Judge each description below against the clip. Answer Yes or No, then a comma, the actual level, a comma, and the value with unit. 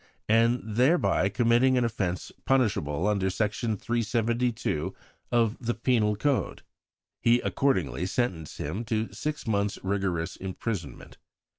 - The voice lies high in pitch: No, low, 110 Hz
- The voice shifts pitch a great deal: No, average, 3.7 semitones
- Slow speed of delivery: Yes, slow, 115 wpm